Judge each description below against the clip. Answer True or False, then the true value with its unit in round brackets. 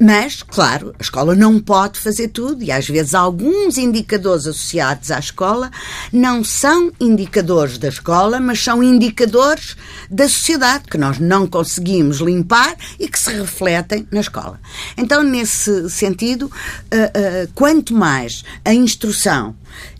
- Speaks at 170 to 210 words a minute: False (130 wpm)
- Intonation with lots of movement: True (6.5 semitones)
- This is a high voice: True (205 Hz)